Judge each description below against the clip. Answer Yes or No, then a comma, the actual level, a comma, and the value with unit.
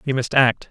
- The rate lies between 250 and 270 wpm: Yes, fast, 255 wpm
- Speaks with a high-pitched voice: No, low, 130 Hz